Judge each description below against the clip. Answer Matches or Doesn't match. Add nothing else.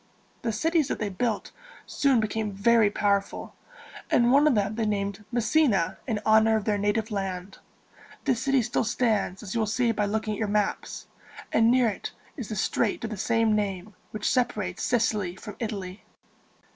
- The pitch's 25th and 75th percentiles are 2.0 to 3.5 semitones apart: Matches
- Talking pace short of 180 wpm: Doesn't match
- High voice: Matches